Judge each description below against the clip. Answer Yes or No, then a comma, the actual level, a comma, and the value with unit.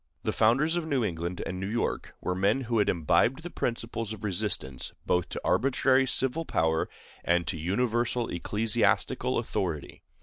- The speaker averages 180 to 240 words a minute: No, average, 160 wpm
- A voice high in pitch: No, low, 110 Hz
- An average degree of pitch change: No, wide, 6.1 semitones